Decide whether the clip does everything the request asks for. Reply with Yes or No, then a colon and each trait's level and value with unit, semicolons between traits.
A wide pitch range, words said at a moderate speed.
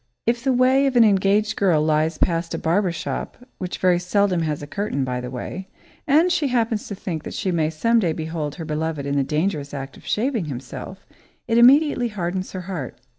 No: wide, 6.3 semitones; fast, 210 wpm